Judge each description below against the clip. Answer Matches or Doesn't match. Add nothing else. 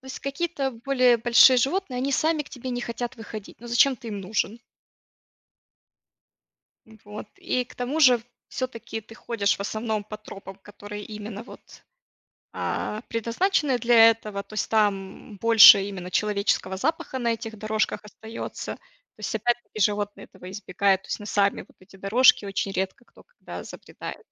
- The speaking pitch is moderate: Doesn't match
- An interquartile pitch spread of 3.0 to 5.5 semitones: Matches